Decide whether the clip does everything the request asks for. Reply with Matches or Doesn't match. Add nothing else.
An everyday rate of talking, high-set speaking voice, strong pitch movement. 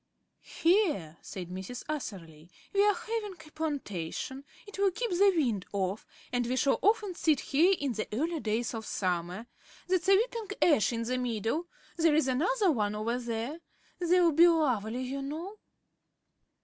Matches